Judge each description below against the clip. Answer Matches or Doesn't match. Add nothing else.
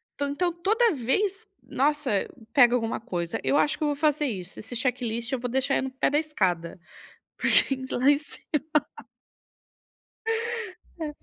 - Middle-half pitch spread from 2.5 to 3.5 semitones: Doesn't match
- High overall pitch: Matches